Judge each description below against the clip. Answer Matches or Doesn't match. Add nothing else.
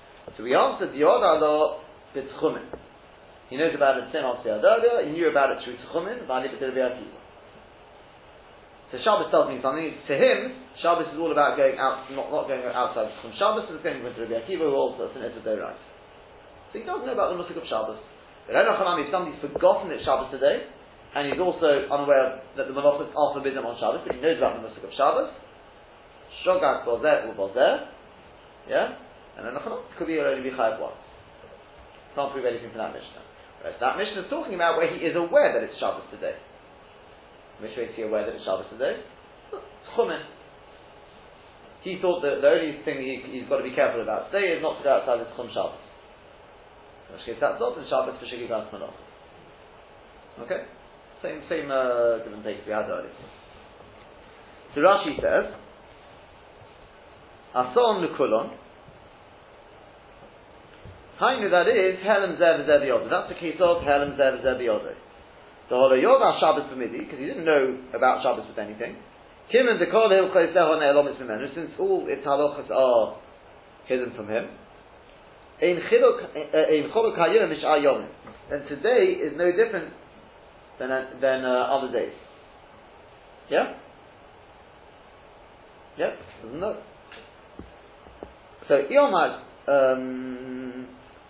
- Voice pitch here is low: Doesn't match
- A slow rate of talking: Doesn't match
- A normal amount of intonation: Doesn't match